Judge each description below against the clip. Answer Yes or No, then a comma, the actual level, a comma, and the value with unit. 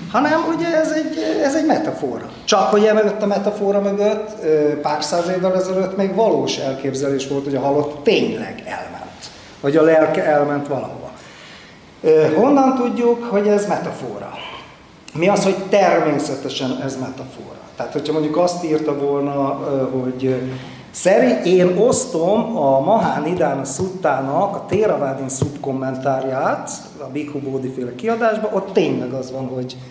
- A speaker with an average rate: Yes, average, 140 wpm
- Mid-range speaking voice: Yes, medium, 150 Hz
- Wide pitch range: Yes, wide, 6.8 semitones